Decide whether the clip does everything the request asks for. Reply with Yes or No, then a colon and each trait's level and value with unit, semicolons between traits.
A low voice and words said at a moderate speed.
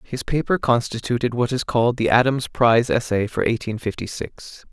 Yes: low, 120 Hz; average, 180 wpm